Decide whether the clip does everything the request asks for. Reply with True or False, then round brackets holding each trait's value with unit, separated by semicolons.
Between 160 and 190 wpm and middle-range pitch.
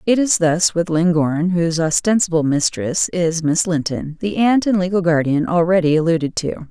True (170 wpm; 170 Hz)